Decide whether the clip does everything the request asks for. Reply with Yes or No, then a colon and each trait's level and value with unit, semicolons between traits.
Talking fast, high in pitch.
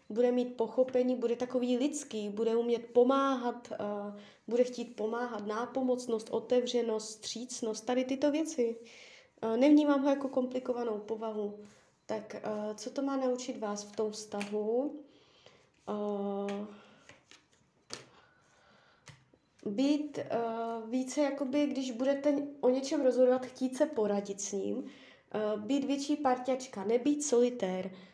No: average, 120 wpm; high, 245 Hz